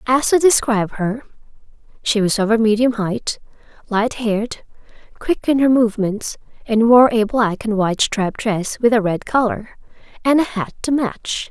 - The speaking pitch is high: Yes, high, 225 Hz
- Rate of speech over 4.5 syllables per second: Yes, 4.9 syllables/s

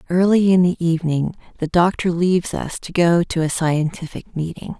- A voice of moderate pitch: Yes, medium, 170 Hz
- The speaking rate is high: No, average, 175 wpm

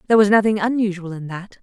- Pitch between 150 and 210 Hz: Yes, high, 200 Hz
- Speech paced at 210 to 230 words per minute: Yes, fast, 220 wpm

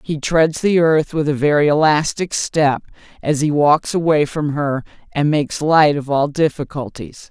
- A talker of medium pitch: Yes, medium, 150 Hz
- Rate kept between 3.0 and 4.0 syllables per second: No, 4.4 syllables/s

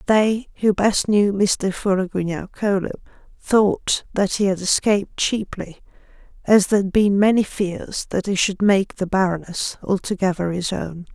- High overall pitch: Yes, high, 195 Hz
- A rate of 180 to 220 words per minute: No, average, 150 wpm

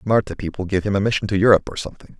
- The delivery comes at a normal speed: No, fast, 275 wpm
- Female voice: No, male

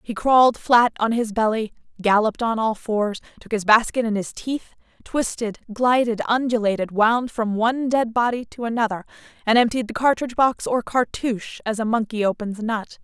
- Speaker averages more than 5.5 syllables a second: No, 5.3 syllables/s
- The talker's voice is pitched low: No, high, 225 Hz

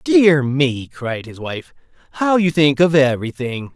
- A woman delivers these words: No, male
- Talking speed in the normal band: Yes, average, 160 wpm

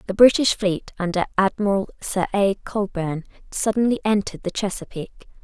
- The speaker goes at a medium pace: No, slow, 130 wpm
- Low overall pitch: No, high, 200 Hz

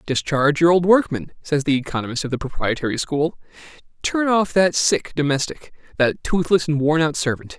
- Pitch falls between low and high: Yes, medium, 155 Hz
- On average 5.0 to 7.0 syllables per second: Yes, 5.4 syllables/s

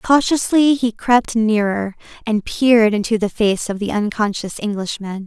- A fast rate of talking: No, average, 150 wpm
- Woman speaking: Yes, female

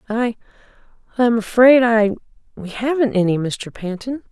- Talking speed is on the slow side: Yes, slow, 95 wpm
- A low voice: No, high, 225 Hz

